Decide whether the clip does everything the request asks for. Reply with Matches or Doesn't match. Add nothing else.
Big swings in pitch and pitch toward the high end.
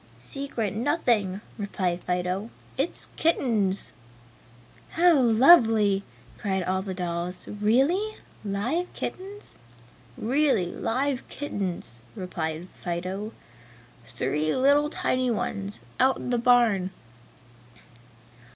Matches